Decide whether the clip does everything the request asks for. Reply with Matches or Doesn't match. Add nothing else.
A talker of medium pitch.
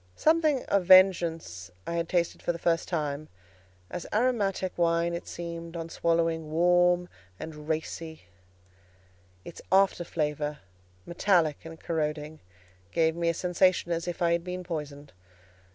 Matches